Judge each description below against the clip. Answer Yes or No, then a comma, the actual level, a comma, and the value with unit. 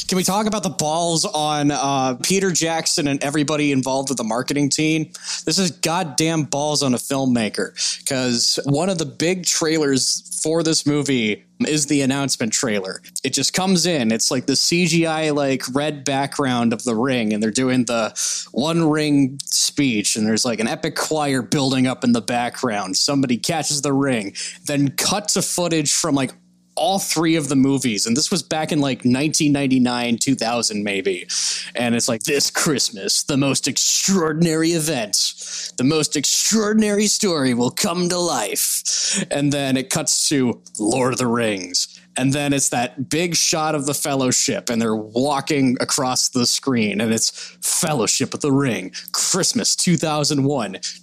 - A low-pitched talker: No, medium, 145 Hz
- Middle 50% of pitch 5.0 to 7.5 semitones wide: No, average, 4.0 semitones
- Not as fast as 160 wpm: No, average, 165 wpm